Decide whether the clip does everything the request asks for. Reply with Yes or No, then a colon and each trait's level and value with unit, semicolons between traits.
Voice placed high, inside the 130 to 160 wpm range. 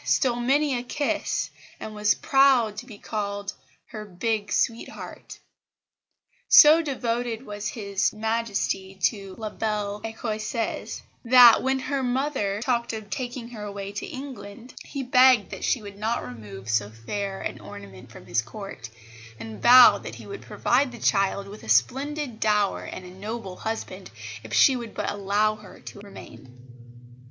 Yes: high, 215 Hz; average, 155 wpm